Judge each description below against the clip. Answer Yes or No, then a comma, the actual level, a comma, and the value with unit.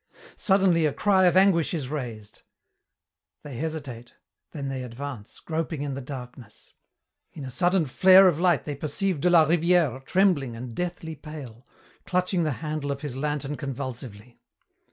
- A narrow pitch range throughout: No, average, 4.8 semitones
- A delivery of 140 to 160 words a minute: Yes, average, 155 wpm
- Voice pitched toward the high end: No, medium, 150 Hz